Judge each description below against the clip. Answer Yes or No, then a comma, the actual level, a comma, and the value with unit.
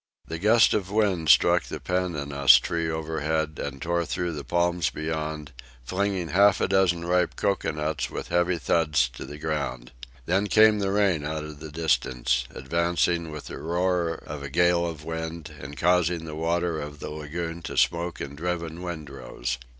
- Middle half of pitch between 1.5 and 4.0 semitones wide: Yes, narrow, 2.6 semitones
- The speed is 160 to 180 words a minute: Yes, average, 170 wpm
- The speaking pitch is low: Yes, very low, 80 Hz